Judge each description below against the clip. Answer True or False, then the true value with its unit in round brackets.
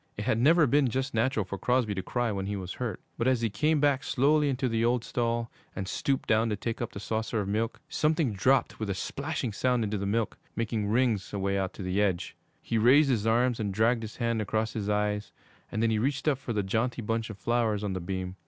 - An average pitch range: True (3.4 semitones)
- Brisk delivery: True (245 wpm)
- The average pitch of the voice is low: True (115 Hz)